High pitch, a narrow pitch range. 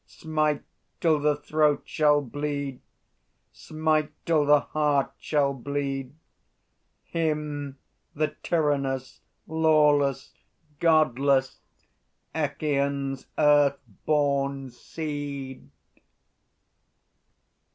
No: medium, 145 Hz; narrow, 1.8 semitones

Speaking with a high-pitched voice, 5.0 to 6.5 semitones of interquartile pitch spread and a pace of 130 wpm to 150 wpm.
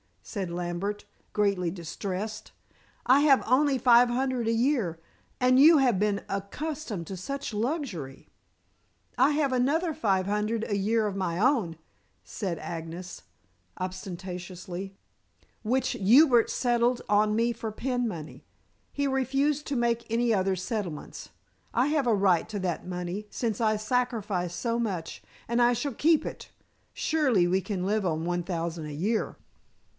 Yes: high, 215 Hz; average, 5.3 semitones; average, 145 wpm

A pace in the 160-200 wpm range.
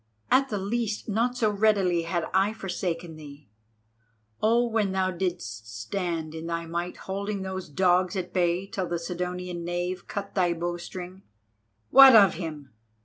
No: average, 150 wpm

